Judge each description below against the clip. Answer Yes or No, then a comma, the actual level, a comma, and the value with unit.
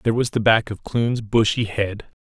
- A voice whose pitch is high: No, low, 110 Hz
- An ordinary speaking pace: No, fast, 215 wpm